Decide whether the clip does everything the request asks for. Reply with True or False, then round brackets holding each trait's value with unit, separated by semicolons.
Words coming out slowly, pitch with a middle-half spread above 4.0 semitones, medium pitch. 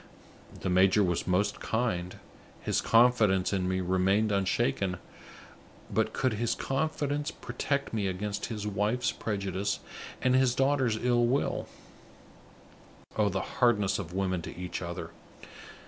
False (130 wpm; 4.7 semitones; 105 Hz)